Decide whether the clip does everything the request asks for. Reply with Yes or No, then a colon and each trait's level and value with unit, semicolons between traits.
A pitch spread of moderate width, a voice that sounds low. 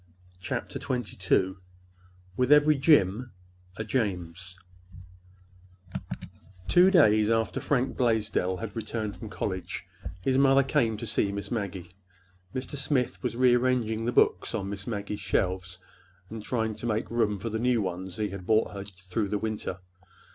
Yes: average, 4.1 semitones; low, 110 Hz